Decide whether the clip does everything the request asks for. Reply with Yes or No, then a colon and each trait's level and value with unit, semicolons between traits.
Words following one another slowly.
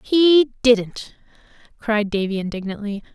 Yes: slow, 95 wpm